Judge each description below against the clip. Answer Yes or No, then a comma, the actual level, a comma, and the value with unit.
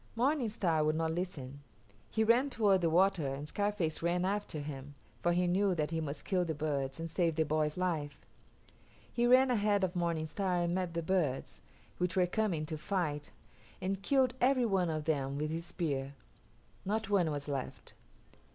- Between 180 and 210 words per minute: Yes, average, 185 wpm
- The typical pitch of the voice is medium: Yes, medium, 175 Hz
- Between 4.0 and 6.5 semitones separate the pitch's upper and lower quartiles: Yes, average, 4.4 semitones